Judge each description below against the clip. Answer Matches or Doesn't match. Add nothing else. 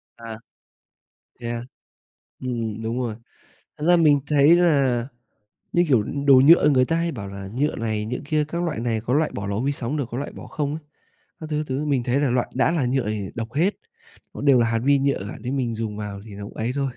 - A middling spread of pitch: Matches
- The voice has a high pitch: Doesn't match